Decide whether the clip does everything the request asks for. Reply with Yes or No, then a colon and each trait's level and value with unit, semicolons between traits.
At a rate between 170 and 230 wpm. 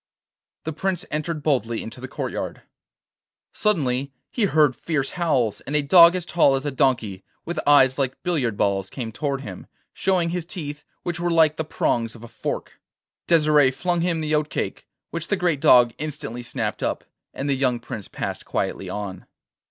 Yes: average, 180 wpm